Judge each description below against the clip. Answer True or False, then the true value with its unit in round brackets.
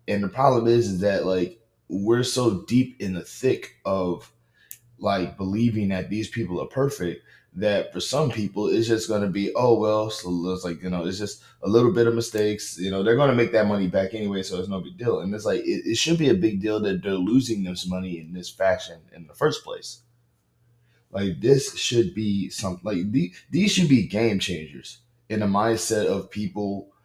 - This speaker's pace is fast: True (215 wpm)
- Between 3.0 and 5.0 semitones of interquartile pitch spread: True (3.8 semitones)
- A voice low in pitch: True (105 Hz)